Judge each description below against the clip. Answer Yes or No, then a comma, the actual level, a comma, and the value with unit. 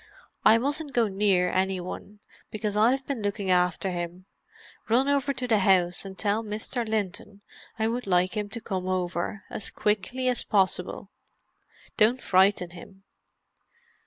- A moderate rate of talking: Yes, average, 145 wpm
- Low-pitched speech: No, high, 205 Hz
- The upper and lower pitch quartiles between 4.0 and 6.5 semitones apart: No, average, 3.4 semitones